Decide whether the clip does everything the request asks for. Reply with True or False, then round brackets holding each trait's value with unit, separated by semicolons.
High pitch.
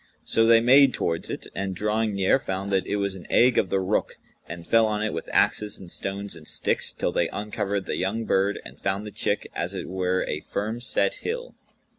False (100 Hz)